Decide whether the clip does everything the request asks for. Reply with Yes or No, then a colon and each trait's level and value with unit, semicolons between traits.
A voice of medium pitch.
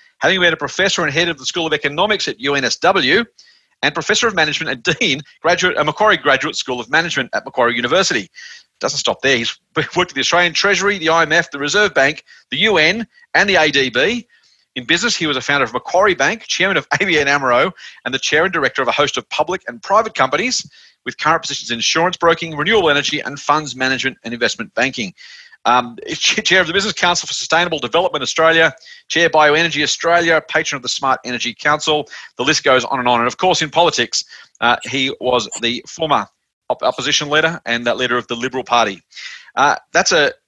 Yes: medium, 160 Hz